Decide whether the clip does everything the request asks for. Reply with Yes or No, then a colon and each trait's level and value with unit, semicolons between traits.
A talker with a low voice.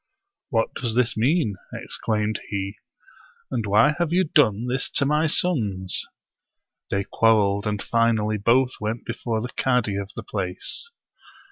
Yes: low, 115 Hz